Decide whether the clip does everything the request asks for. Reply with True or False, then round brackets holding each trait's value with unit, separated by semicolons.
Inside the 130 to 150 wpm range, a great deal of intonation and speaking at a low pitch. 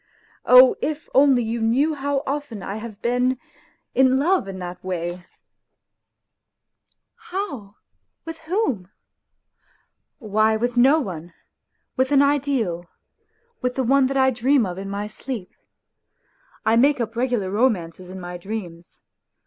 False (145 wpm; 5.7 semitones; 235 Hz)